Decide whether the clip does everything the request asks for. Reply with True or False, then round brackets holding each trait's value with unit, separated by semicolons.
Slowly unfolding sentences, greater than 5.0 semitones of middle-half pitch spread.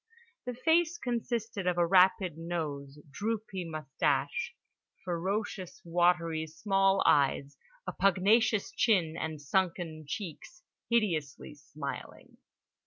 True (100 wpm; 5.5 semitones)